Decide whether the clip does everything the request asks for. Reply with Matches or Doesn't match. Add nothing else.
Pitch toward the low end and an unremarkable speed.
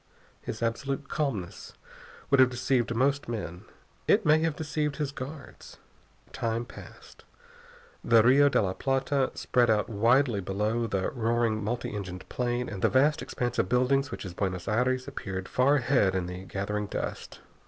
Matches